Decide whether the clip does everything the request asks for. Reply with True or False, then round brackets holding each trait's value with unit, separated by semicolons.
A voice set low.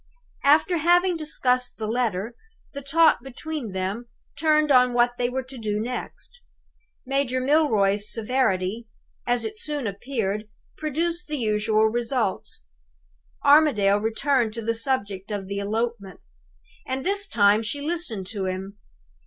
False (240 Hz)